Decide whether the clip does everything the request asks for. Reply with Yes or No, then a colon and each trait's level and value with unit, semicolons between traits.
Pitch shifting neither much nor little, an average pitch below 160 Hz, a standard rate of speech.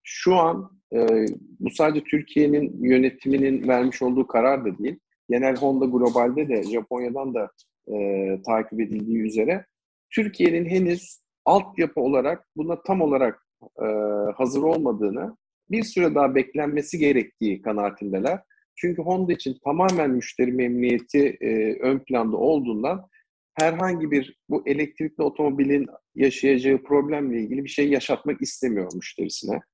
Yes: average, 5.0 semitones; medium, 140 Hz; average, 125 wpm